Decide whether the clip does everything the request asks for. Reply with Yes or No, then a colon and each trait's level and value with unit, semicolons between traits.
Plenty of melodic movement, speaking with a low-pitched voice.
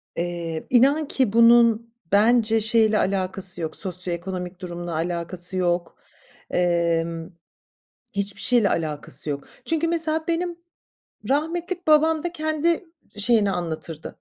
No: wide, 8.7 semitones; high, 200 Hz